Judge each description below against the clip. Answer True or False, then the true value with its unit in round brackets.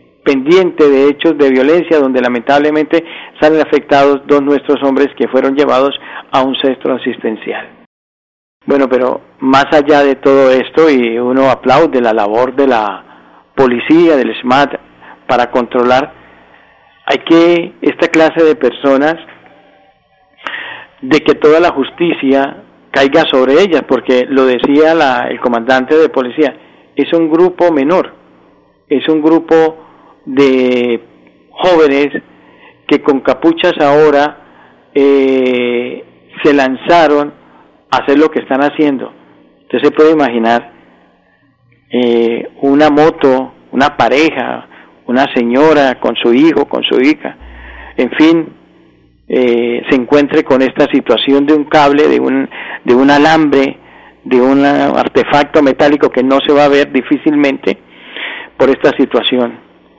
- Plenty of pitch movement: False (3.0 semitones)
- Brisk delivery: False (130 wpm)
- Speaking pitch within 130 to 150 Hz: True (140 Hz)